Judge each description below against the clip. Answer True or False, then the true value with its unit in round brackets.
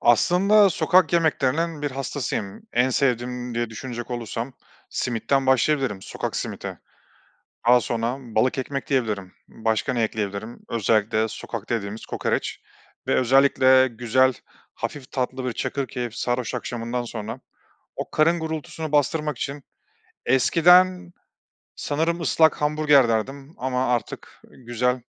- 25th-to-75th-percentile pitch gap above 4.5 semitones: False (3.8 semitones)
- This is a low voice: True (130 Hz)